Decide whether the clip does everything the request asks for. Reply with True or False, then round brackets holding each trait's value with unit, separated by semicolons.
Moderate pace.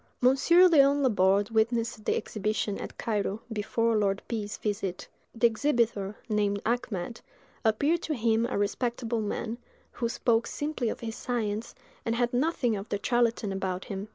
True (155 wpm)